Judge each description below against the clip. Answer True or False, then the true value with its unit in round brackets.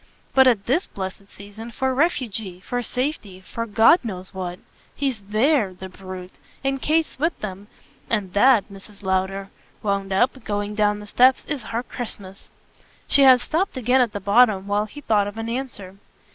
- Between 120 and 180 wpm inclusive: True (175 wpm)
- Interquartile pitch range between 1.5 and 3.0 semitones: False (4.7 semitones)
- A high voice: True (215 Hz)